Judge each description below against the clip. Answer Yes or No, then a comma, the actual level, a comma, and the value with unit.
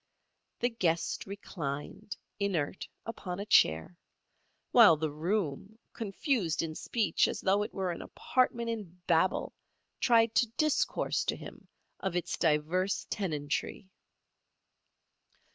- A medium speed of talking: No, slow, 115 wpm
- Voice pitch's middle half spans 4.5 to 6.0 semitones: Yes, average, 5.0 semitones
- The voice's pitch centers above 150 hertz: Yes, high, 190 Hz